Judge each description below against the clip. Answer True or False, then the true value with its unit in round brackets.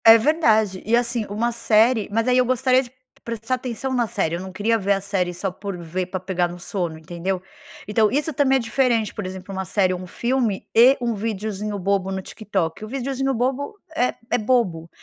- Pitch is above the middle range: True (215 Hz)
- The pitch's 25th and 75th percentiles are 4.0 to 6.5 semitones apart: True (4.4 semitones)